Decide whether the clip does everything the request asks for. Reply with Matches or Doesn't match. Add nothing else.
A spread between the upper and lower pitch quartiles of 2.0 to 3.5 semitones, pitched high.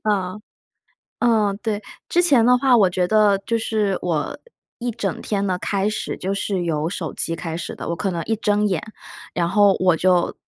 Matches